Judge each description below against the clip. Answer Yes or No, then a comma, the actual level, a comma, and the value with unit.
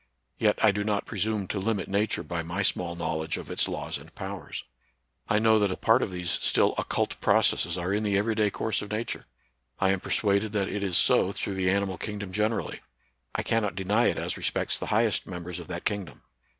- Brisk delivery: Yes, fast, 215 wpm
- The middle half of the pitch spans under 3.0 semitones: Yes, narrow, 2.5 semitones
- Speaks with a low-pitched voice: Yes, low, 100 Hz